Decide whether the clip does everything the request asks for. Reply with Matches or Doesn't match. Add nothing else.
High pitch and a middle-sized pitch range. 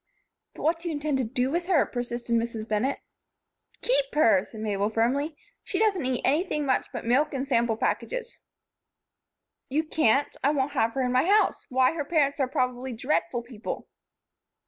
Matches